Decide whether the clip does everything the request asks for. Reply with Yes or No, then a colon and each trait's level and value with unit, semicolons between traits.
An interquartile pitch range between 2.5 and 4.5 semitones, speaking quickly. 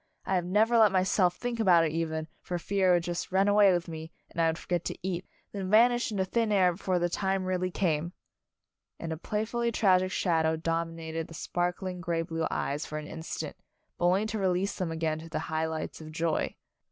Yes: average, 2.8 semitones; fast, 215 wpm